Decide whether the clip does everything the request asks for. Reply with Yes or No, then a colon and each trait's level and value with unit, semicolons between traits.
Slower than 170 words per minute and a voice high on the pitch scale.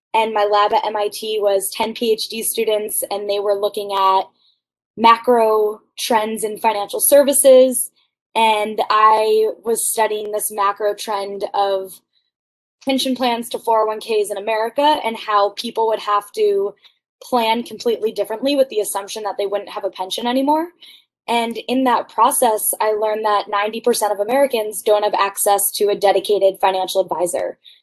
Yes: average, 150 wpm; high, 215 Hz